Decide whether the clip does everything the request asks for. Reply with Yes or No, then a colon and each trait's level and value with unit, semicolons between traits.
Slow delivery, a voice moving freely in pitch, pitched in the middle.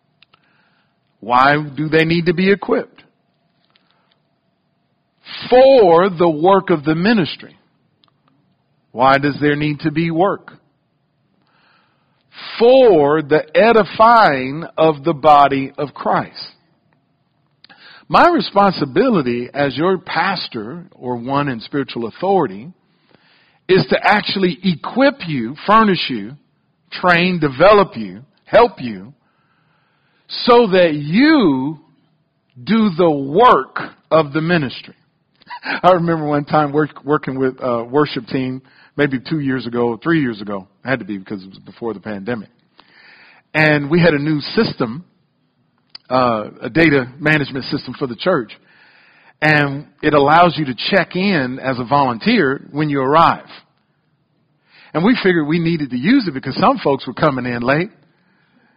No: slow, 130 wpm; average, 4.8 semitones; medium, 155 Hz